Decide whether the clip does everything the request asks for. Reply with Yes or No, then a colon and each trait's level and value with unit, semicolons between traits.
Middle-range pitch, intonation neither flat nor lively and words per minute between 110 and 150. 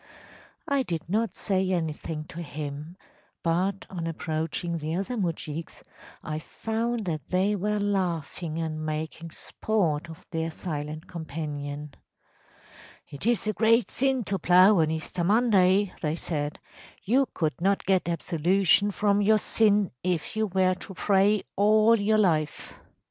Yes: medium, 180 Hz; average, 4.4 semitones; average, 140 wpm